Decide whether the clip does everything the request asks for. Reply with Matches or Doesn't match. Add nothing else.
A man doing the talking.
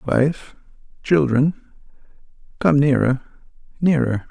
Matches